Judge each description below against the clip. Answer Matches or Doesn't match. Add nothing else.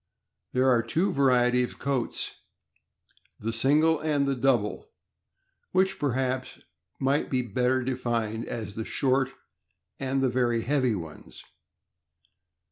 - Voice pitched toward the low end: Matches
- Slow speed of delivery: Matches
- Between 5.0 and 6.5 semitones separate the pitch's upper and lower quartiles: Doesn't match